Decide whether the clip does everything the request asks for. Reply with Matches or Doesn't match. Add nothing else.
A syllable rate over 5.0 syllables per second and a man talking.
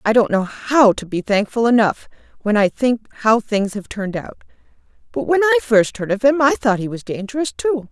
Doesn't match